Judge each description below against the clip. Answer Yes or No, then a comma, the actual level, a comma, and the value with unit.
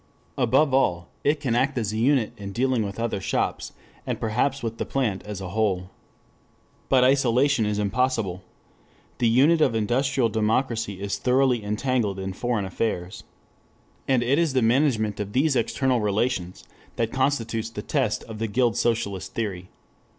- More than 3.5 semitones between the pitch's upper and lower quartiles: Yes, average, 4.1 semitones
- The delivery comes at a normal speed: Yes, average, 160 wpm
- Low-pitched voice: Yes, low, 115 Hz